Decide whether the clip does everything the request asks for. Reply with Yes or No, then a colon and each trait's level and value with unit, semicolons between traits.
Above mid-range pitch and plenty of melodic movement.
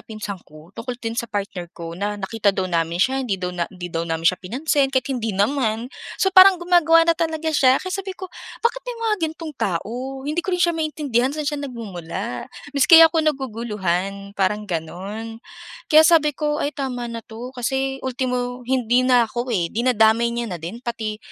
Yes: high, 240 Hz; wide, 6.4 semitones